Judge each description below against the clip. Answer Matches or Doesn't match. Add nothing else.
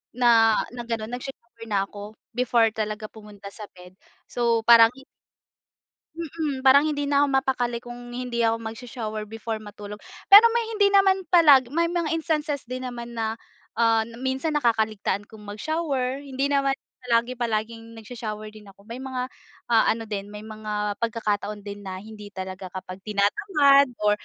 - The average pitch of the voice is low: Doesn't match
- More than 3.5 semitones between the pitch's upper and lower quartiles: Matches